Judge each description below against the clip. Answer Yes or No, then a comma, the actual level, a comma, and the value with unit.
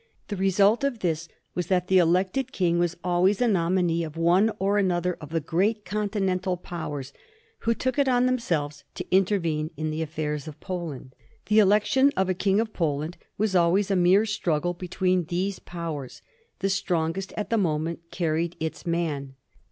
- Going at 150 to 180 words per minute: Yes, average, 175 wpm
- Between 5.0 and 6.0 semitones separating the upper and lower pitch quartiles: No, average, 3.3 semitones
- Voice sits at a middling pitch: Yes, medium, 180 Hz